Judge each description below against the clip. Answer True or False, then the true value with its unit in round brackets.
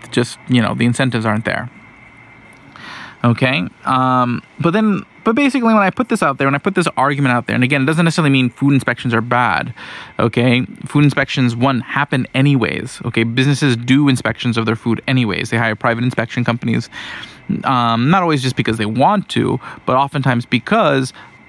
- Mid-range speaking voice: False (130 Hz)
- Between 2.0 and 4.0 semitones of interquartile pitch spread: True (3.0 semitones)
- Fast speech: False (185 wpm)